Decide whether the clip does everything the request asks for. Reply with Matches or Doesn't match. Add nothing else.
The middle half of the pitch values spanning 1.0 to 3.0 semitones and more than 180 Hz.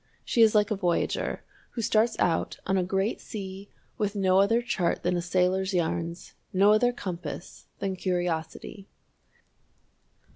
Matches